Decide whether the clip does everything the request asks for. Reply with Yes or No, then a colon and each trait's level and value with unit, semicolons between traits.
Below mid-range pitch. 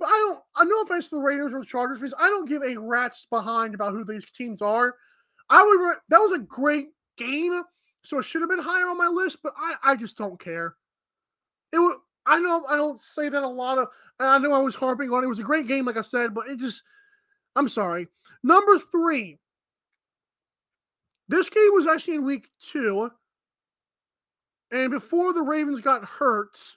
No: very high, 280 Hz